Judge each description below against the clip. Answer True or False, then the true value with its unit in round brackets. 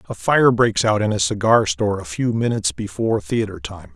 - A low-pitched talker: True (105 Hz)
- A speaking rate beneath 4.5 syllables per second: False (5.6 syllables/s)